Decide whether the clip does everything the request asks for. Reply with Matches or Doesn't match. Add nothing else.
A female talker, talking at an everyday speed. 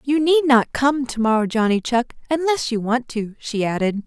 Matches